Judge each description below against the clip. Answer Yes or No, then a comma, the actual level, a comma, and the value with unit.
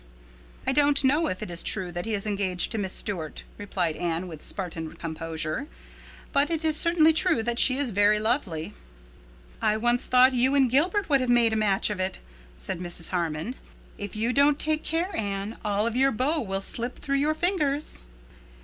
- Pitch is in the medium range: No, high, 225 Hz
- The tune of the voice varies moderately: No, wide, 7.0 semitones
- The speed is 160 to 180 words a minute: No, average, 195 wpm